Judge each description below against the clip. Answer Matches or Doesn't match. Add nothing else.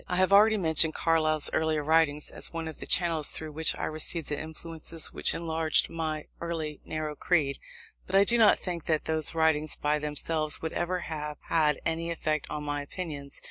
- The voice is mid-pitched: Matches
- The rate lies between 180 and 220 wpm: Matches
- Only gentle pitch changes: Matches